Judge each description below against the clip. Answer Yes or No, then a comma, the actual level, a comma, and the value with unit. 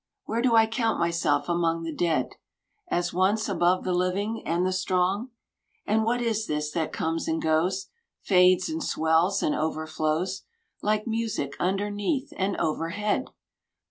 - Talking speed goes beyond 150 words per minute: No, average, 145 wpm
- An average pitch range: Yes, average, 4.4 semitones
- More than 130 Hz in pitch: Yes, medium, 185 Hz